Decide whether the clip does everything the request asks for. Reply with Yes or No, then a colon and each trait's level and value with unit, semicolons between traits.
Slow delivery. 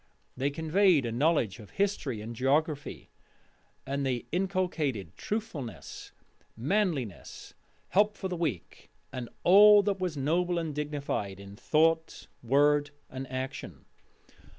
Yes: slow, 120 wpm